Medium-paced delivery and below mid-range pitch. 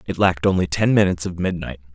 No: fast, 215 wpm; very low, 90 Hz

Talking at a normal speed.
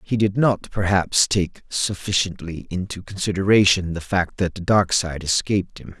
Yes: average, 160 wpm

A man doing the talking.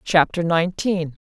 No: female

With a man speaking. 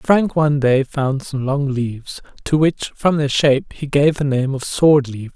Yes: male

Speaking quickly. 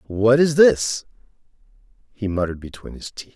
No: average, 145 wpm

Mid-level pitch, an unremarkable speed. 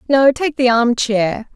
No: high, 245 Hz; average, 195 wpm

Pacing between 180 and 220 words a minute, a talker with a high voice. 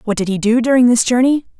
No: fast, 265 wpm; high, 235 Hz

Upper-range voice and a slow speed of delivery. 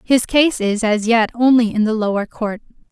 No: high, 225 Hz; fast, 205 wpm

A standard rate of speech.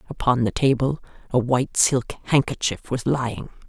Yes: average, 145 wpm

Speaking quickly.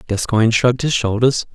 No: average, 155 wpm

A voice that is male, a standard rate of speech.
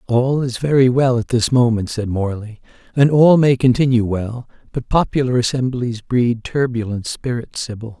Yes: male; average, 160 wpm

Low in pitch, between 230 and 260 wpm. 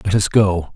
Yes: very low, 95 Hz; fast, 235 wpm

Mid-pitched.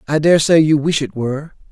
Yes: medium, 150 Hz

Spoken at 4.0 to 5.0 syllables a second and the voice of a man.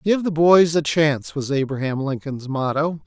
Yes: 4.8 syllables/s; male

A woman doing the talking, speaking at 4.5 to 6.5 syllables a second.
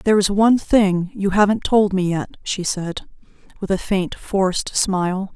Yes: female; 4.6 syllables/s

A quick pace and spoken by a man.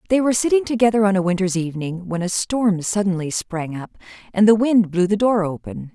No: fast, 210 wpm; female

